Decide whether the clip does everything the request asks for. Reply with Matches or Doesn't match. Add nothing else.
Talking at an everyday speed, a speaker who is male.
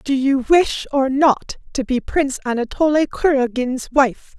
Doesn't match